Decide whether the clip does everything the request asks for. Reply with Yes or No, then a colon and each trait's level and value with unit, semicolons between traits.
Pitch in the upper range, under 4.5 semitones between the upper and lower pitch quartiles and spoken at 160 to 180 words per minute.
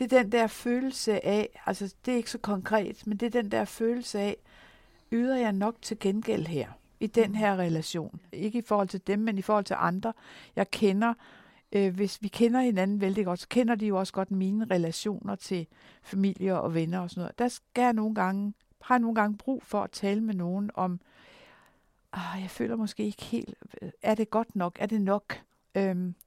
No: high, 205 Hz; average, 3.0 semitones; average, 210 wpm